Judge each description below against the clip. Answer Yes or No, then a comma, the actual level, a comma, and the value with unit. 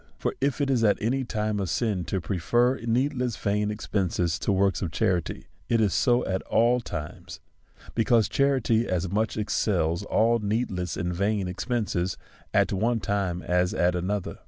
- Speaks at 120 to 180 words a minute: Yes, average, 165 wpm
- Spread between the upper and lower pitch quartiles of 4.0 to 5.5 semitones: Yes, average, 4.4 semitones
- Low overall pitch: Yes, low, 105 Hz